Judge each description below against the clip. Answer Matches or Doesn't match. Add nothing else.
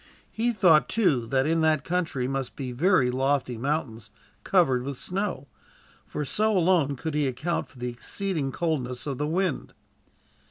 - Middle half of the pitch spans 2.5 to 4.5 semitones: Doesn't match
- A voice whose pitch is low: Doesn't match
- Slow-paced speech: Doesn't match